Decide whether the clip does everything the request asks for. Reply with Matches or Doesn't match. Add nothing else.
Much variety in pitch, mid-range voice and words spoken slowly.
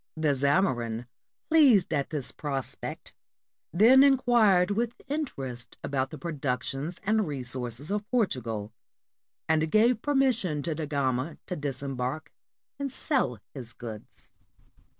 Matches